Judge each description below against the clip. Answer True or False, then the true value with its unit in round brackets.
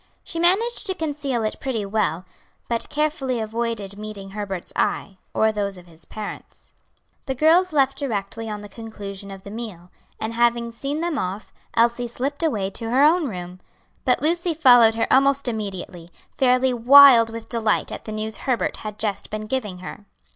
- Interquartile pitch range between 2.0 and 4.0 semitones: False (4.8 semitones)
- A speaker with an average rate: True (175 wpm)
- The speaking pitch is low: False (230 Hz)